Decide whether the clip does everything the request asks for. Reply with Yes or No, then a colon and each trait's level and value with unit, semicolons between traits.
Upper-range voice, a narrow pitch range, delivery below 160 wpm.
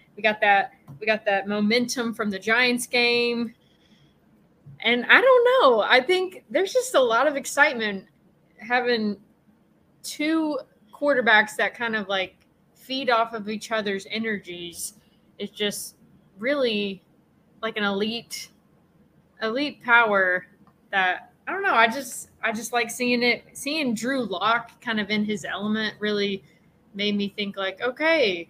No: high, 225 Hz; average, 3.4 semitones; average, 145 wpm